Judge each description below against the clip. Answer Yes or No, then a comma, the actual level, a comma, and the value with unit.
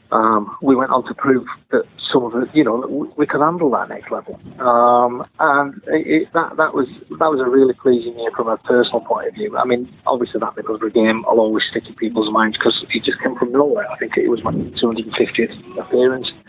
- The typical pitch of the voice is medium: No, low, 120 Hz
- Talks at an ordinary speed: No, fast, 235 wpm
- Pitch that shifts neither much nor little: No, narrow, 2.2 semitones